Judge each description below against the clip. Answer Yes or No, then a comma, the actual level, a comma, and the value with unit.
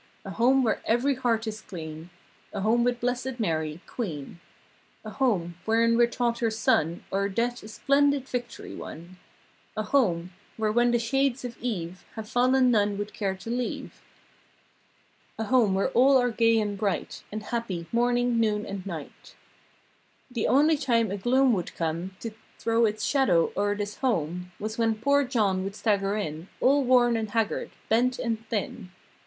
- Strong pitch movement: No, average, 3.8 semitones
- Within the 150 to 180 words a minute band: Yes, average, 170 wpm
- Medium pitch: No, high, 225 Hz